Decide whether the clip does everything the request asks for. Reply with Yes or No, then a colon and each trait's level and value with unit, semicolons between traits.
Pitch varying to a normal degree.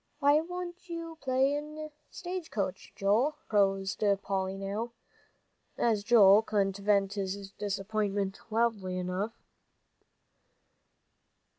No: wide, 6.6 semitones